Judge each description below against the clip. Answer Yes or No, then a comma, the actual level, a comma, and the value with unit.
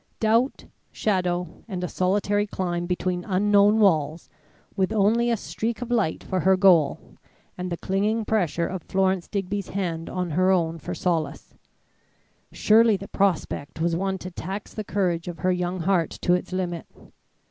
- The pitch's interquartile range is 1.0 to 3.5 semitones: Yes, narrow, 2.6 semitones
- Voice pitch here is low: No, medium, 185 Hz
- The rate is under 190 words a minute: Yes, average, 160 wpm